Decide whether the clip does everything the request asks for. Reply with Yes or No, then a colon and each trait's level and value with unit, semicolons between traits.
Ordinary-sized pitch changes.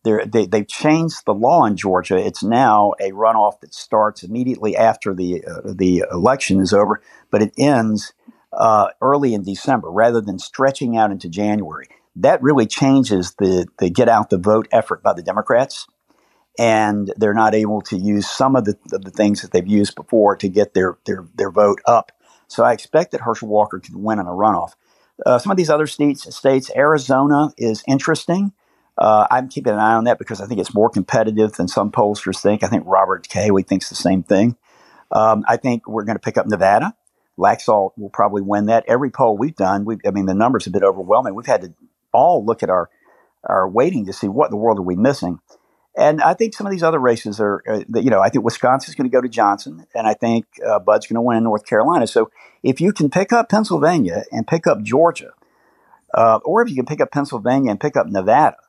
Yes: average, 4.7 semitones